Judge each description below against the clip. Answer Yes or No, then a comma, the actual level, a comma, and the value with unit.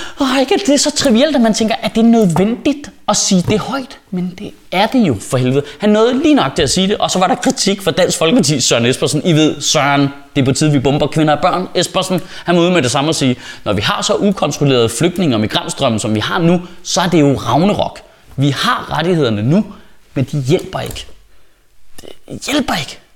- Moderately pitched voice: Yes, medium, 180 Hz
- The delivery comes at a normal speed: No, fast, 245 wpm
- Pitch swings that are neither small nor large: No, wide, 6.6 semitones